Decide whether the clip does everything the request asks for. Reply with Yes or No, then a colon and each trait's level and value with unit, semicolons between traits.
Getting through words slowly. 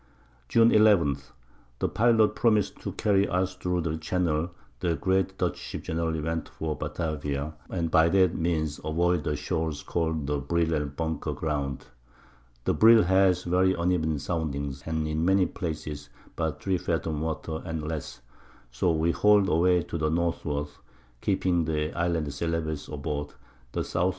No: average, 155 wpm